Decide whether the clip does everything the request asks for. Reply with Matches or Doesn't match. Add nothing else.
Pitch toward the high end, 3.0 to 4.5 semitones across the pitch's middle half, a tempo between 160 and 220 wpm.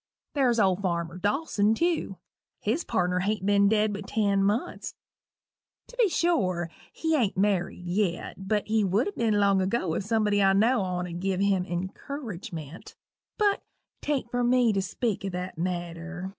Matches